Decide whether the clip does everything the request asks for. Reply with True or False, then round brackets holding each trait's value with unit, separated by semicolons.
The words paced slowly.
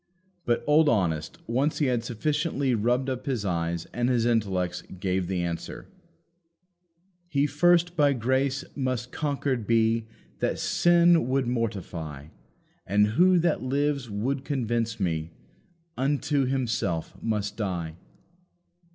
True (125 wpm)